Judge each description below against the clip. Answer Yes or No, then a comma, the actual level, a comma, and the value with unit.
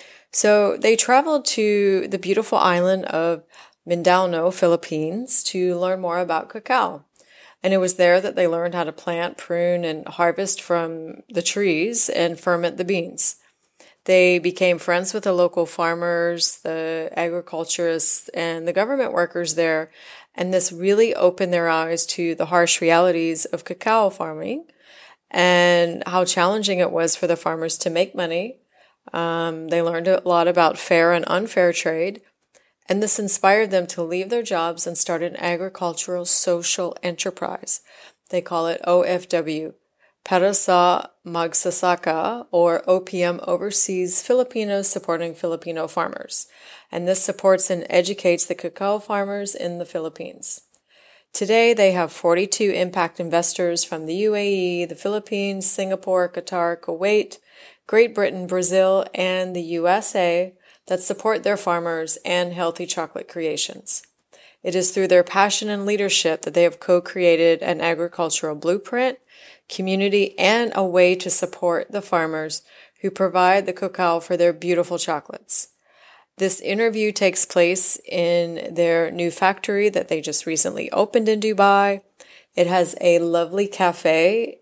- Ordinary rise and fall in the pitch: No, narrow, 2.2 semitones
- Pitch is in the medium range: Yes, medium, 180 Hz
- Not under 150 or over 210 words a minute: No, average, 140 wpm